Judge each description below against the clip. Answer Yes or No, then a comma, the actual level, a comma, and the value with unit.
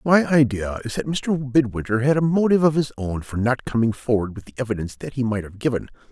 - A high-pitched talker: No, low, 125 Hz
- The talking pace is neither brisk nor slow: No, fast, 235 wpm